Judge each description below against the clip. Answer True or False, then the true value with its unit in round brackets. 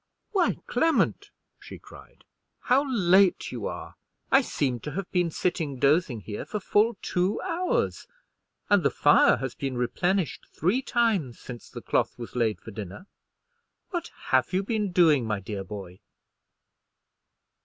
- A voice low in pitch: False (175 Hz)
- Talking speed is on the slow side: False (145 wpm)